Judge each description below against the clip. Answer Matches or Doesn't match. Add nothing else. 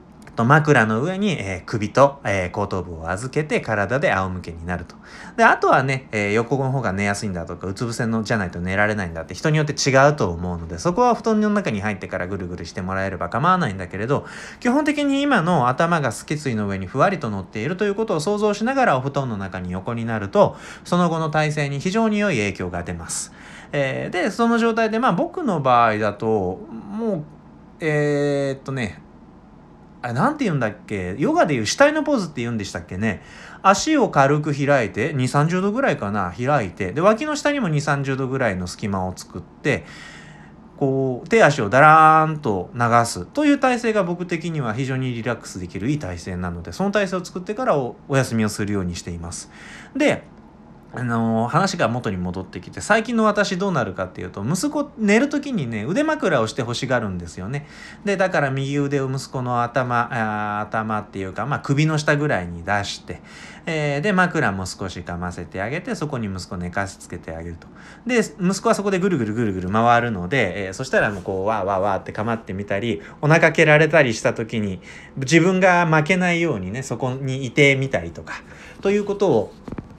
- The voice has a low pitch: Matches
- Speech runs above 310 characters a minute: Matches